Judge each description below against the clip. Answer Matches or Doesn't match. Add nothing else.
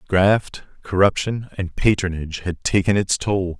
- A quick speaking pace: Doesn't match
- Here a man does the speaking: Matches